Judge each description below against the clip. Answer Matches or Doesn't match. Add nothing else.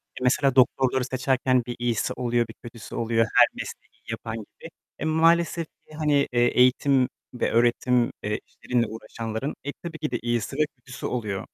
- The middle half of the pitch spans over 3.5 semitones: Doesn't match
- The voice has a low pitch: Matches